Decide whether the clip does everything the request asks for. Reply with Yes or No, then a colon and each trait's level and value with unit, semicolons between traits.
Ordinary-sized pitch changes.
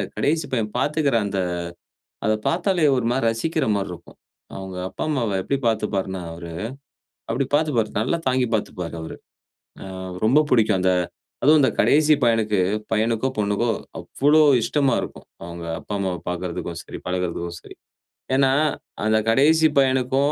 No: wide, 6.4 semitones